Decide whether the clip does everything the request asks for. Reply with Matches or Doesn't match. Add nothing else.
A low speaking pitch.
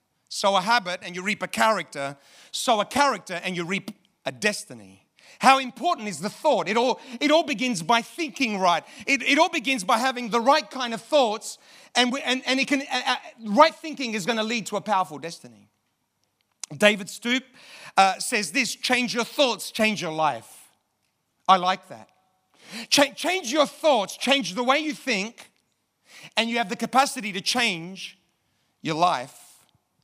Doesn't match